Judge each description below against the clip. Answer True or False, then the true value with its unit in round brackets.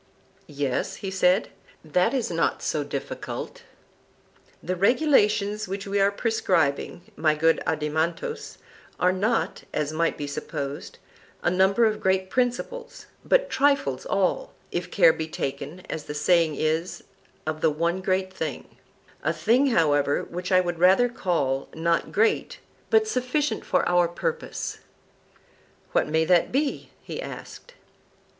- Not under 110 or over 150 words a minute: True (135 wpm)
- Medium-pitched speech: True (180 Hz)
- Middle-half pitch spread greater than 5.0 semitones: True (5.4 semitones)